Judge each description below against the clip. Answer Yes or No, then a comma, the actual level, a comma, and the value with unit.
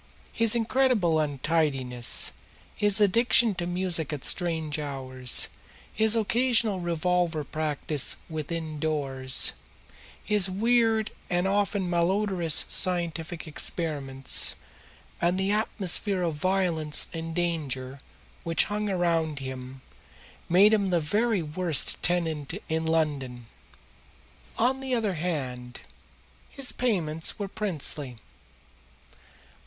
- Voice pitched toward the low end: No, medium, 170 Hz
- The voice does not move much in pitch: No, average, 5.0 semitones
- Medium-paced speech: No, slow, 100 wpm